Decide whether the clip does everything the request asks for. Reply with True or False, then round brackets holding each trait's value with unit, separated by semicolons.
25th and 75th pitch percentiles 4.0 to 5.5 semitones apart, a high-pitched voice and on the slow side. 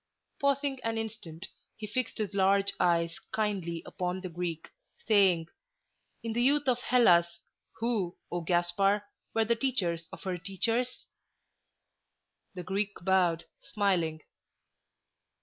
True (4.6 semitones; 195 Hz; 120 wpm)